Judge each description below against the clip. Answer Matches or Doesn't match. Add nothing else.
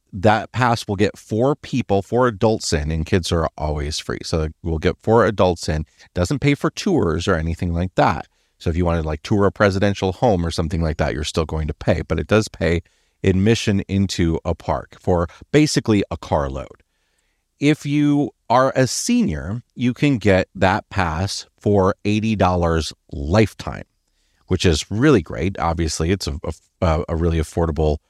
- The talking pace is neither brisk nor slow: Matches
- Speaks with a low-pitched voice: Matches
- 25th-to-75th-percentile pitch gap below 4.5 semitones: Doesn't match